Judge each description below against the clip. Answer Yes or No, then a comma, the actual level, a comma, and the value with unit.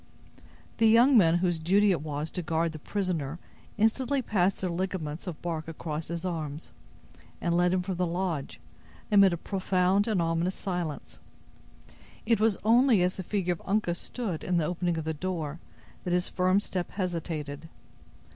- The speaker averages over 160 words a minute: Yes, average, 170 wpm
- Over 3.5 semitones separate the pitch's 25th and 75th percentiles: No, average, 3.0 semitones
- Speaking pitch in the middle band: Yes, medium, 180 Hz